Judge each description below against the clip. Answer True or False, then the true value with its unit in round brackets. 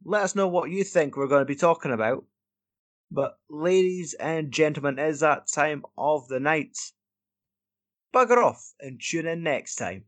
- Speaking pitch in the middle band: True (150 Hz)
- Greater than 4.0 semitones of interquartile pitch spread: True (4.5 semitones)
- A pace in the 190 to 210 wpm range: False (180 wpm)